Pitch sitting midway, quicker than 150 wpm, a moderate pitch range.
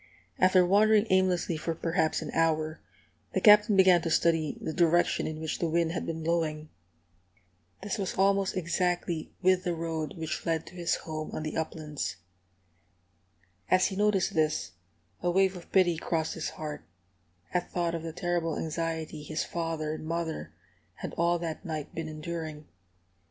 No: medium, 165 Hz; average, 160 wpm; narrow, 2.2 semitones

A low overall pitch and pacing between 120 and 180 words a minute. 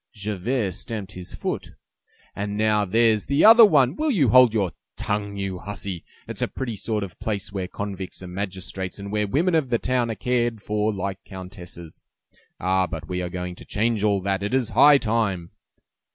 No: low, 105 Hz; average, 195 wpm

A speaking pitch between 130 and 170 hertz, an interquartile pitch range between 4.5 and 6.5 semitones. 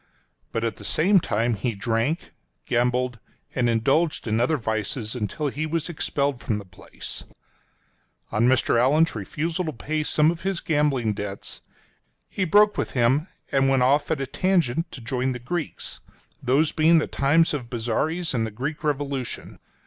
Yes: low, 135 Hz; average, 5.0 semitones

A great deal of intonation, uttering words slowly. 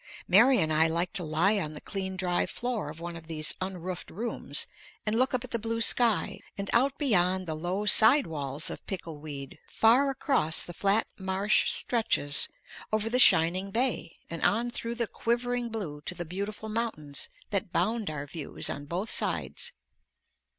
No: wide, 5.9 semitones; average, 180 wpm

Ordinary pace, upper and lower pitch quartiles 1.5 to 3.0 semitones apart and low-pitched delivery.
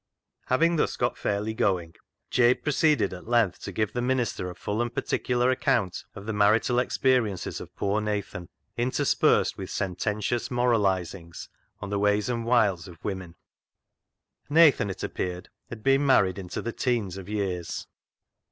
No: average, 160 wpm; average, 4.3 semitones; low, 105 Hz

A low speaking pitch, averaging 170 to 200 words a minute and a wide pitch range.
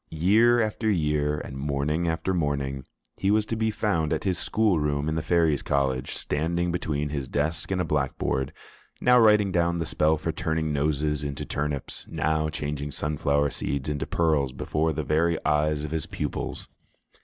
No: very low, 75 Hz; average, 175 wpm; average, 2.9 semitones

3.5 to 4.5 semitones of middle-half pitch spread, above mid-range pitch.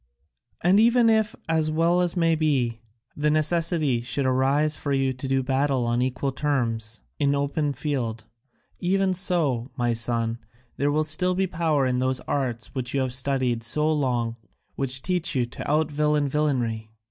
No: average, 3.8 semitones; medium, 140 Hz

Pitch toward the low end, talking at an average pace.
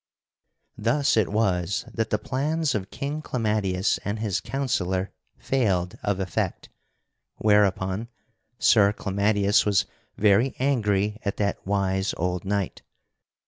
No: low, 105 Hz; slow, 115 wpm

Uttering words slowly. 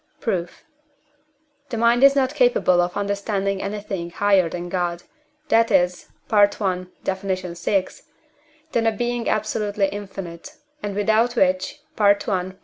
Yes: slow, 125 wpm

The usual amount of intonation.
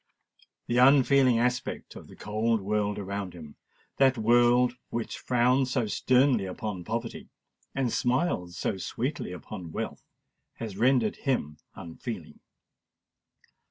Yes: average, 4.0 semitones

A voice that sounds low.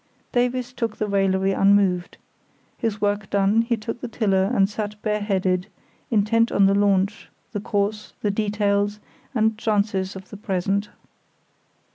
No: high, 205 Hz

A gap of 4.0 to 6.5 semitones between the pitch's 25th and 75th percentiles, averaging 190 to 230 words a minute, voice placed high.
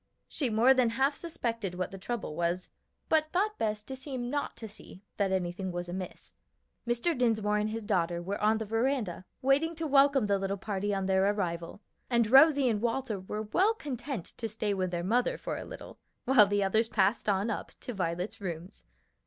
Yes: average, 5.0 semitones; average, 195 wpm; high, 215 Hz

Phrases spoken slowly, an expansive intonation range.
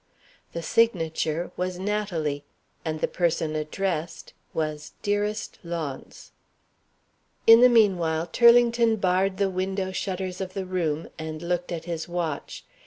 No: slow, 125 wpm; average, 3.5 semitones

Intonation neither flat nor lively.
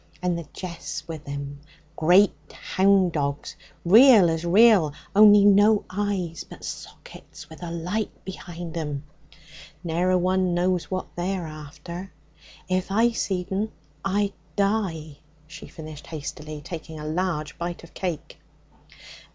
Yes: average, 3.4 semitones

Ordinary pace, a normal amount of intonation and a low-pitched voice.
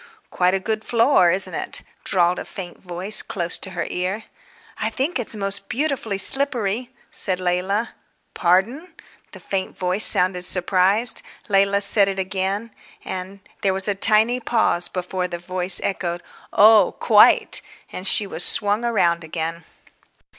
No: average, 145 wpm; average, 3.1 semitones; high, 195 Hz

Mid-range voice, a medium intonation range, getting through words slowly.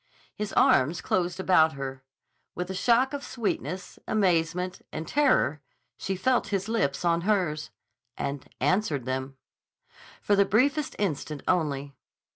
No: medium, 180 Hz; wide, 6.1 semitones; slow, 125 wpm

